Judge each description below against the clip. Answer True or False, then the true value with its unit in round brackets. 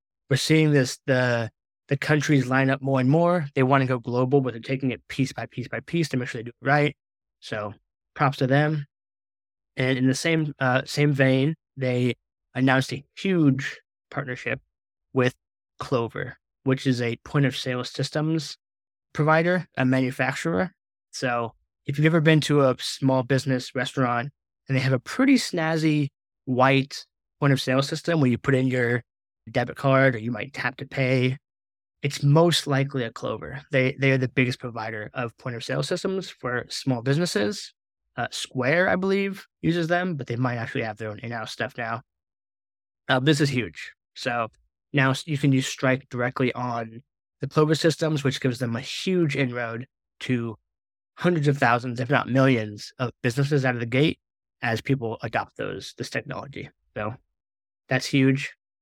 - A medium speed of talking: True (175 wpm)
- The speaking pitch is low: True (130 Hz)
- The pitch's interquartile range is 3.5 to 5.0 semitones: False (2.9 semitones)